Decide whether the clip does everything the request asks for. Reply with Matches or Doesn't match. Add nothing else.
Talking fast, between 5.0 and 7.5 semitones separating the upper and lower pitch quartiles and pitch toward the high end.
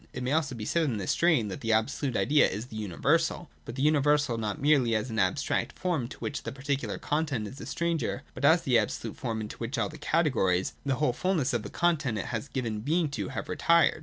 Doesn't match